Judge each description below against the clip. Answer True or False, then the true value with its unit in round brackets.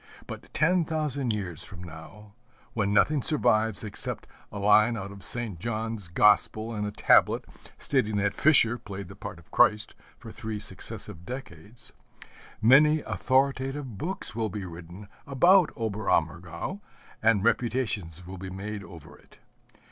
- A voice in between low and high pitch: False (105 Hz)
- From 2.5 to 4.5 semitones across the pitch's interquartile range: True (4.2 semitones)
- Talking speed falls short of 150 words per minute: True (140 wpm)